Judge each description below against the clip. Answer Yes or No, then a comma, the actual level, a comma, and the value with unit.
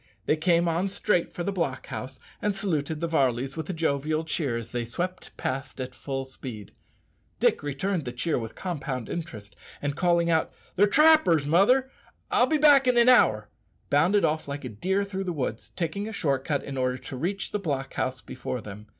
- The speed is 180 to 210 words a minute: Yes, average, 200 wpm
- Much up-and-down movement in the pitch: Yes, wide, 6.1 semitones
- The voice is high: No, medium, 155 Hz